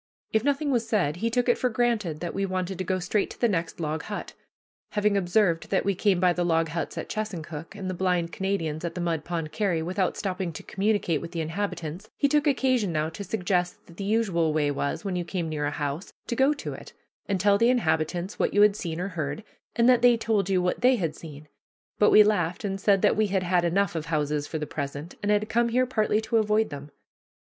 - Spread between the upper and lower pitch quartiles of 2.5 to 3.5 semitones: No, average, 4.4 semitones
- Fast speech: Yes, fast, 240 wpm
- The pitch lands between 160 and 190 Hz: Yes, medium, 185 Hz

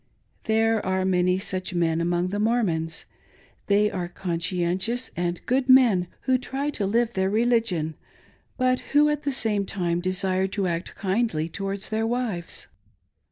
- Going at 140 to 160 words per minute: Yes, average, 155 wpm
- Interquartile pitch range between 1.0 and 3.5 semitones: No, average, 4.6 semitones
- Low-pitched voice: No, high, 195 Hz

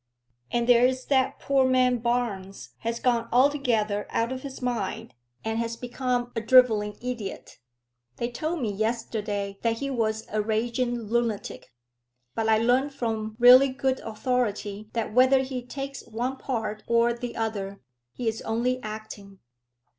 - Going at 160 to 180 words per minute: No, average, 150 wpm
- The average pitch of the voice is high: Yes, high, 235 Hz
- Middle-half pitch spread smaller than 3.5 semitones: Yes, narrow, 2.6 semitones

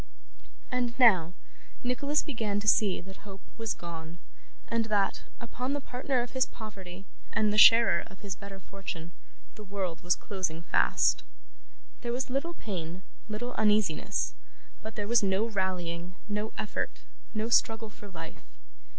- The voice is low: No, high, 210 Hz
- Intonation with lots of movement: No, average, 3.7 semitones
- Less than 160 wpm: Yes, average, 150 wpm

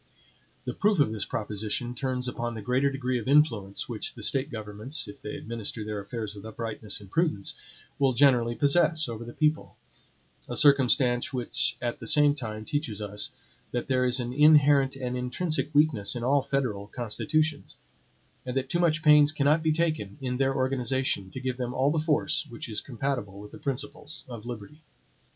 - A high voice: No, low, 125 Hz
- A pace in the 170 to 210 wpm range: Yes, average, 180 wpm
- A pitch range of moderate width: Yes, average, 4.2 semitones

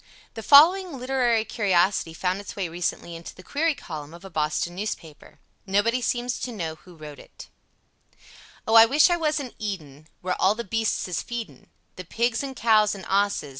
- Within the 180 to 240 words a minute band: Yes, average, 185 wpm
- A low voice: No, high, 205 Hz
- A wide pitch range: Yes, wide, 5.7 semitones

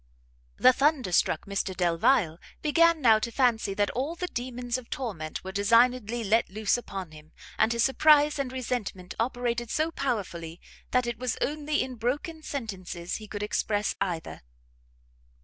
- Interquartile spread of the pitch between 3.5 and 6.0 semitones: Yes, average, 4.8 semitones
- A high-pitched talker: Yes, high, 235 Hz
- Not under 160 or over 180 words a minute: No, average, 150 wpm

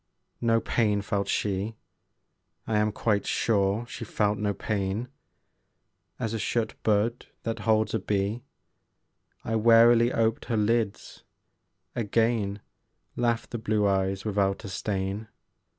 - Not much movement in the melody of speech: Yes, narrow, 2.2 semitones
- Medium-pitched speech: No, low, 110 Hz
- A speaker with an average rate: No, slow, 125 wpm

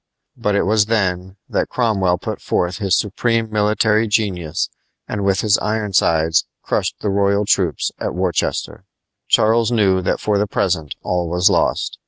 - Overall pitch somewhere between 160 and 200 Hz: No, low, 100 Hz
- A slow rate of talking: No, average, 155 wpm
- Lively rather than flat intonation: No, average, 3.0 semitones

